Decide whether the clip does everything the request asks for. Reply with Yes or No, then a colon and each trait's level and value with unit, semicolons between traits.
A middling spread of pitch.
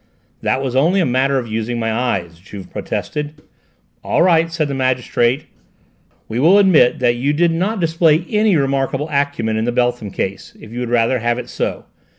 Yes: average, 5.0 semitones